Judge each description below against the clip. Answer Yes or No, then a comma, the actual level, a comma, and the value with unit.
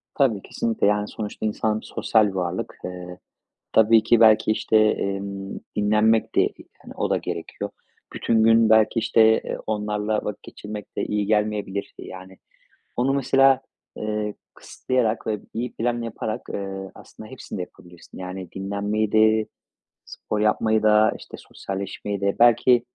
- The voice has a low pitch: Yes, low, 105 Hz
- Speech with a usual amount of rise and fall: No, narrow, 1.9 semitones